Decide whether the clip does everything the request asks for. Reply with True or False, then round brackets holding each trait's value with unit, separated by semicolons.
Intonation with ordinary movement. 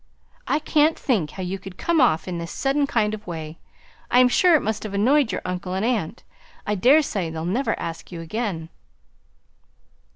False (6.5 semitones)